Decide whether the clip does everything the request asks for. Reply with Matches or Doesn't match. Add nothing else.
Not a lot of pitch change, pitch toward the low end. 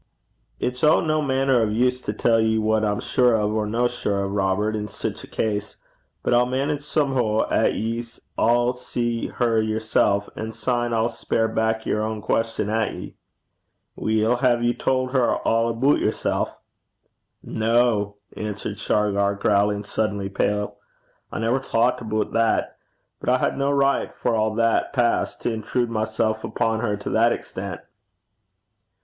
Matches